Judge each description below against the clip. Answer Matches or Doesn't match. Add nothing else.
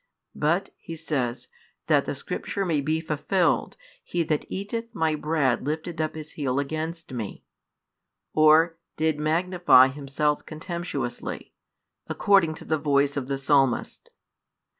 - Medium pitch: Matches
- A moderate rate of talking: Doesn't match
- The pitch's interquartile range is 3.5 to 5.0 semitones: Doesn't match